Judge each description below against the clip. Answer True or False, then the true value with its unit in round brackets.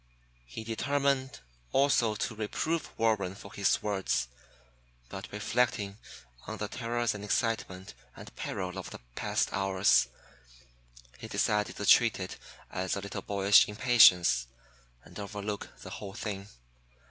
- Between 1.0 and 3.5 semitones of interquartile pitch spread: True (2.9 semitones)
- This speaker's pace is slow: True (130 wpm)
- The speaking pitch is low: True (105 Hz)